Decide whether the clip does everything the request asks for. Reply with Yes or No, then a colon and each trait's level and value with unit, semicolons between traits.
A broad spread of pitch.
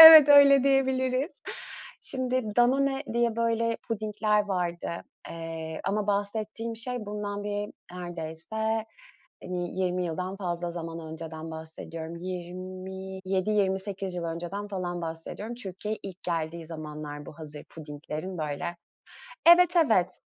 No: average, 4.8 semitones